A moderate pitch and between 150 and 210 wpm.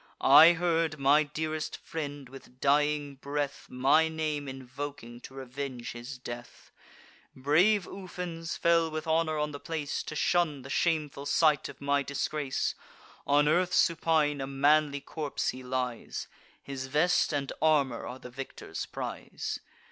No: medium, 145 Hz; average, 140 wpm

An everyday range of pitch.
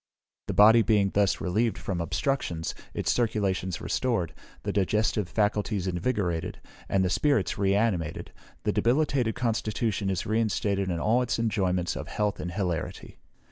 Yes: average, 3.5 semitones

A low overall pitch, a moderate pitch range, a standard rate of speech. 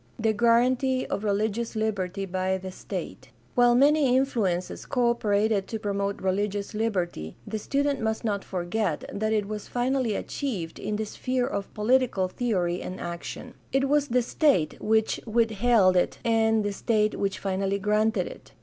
No: high, 215 Hz; average, 3.5 semitones; average, 160 wpm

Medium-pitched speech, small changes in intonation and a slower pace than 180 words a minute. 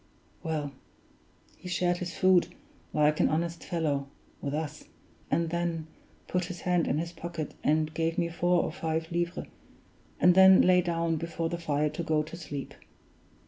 Yes: medium, 165 Hz; narrow, 2.0 semitones; average, 165 wpm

